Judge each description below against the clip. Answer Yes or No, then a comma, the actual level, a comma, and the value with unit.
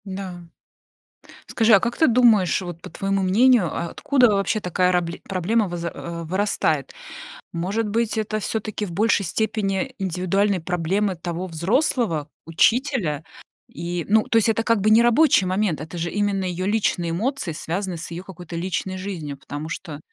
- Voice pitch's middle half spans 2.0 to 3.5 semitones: No, average, 4.1 semitones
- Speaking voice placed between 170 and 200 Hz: Yes, high, 190 Hz